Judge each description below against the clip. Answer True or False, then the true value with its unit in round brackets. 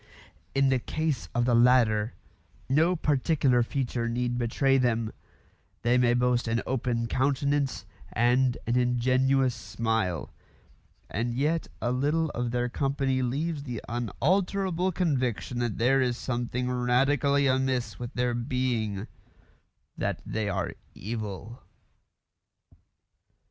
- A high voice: False (125 Hz)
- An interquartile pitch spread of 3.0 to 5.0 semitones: False (2.4 semitones)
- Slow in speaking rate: True (115 wpm)